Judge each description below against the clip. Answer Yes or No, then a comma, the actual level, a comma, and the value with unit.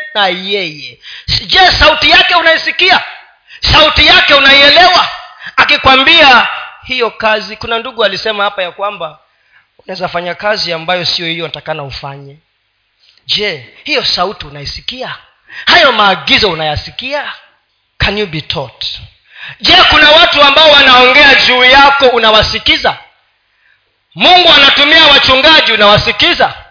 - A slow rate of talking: Yes, slow, 95 wpm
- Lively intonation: Yes, wide, 8.9 semitones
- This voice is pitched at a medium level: No, high, 225 Hz